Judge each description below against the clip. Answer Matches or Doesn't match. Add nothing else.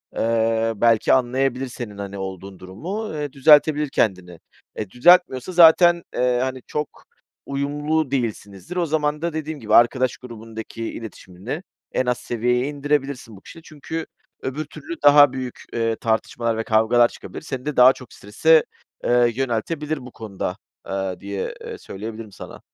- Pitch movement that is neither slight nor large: Matches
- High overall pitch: Doesn't match